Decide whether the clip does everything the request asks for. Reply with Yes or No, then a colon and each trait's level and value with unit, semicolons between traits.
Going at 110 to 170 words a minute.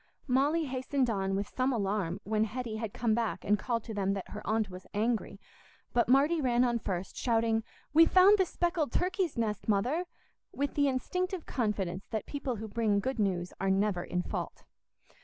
No: average, 185 wpm